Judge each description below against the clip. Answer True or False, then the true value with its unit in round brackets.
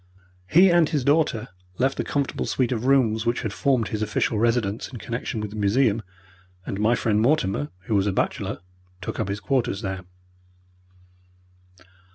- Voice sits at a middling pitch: False (115 Hz)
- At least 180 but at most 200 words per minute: False (170 wpm)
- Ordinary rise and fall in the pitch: True (4.2 semitones)